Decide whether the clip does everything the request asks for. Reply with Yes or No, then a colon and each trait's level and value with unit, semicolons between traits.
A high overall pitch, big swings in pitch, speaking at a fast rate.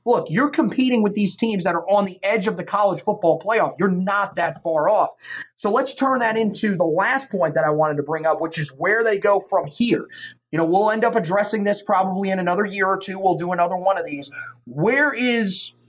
No: high, 200 Hz; average, 4.0 semitones; fast, 240 wpm